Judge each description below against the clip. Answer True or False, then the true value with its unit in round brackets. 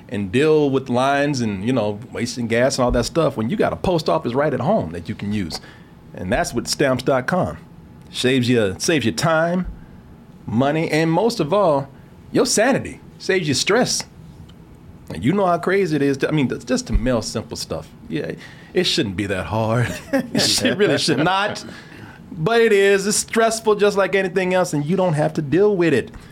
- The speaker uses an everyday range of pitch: False (7.9 semitones)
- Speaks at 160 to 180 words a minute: False (200 wpm)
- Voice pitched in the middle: True (145 Hz)